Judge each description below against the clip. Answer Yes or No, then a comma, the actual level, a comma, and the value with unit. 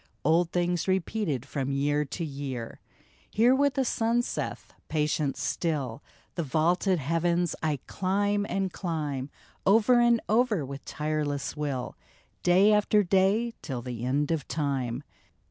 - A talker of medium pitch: Yes, medium, 165 Hz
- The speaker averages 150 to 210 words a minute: No, average, 140 wpm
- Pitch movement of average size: No, wide, 5.8 semitones